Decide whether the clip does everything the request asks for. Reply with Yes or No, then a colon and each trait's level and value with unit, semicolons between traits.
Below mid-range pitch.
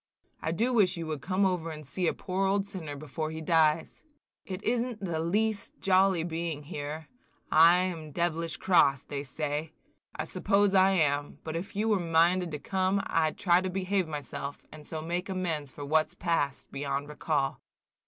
No: medium, 165 Hz